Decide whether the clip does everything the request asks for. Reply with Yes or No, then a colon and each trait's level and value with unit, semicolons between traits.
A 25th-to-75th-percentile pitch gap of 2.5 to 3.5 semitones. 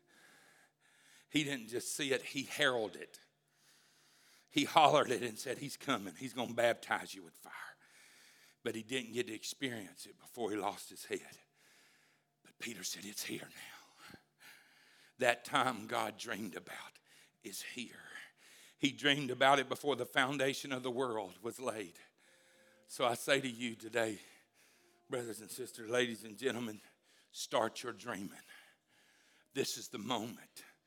Yes: average, 2.8 semitones